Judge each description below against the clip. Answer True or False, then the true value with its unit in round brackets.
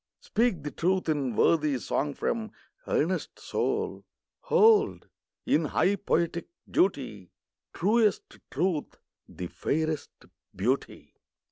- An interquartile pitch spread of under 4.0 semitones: False (5.3 semitones)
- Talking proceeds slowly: True (100 wpm)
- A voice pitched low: False (160 Hz)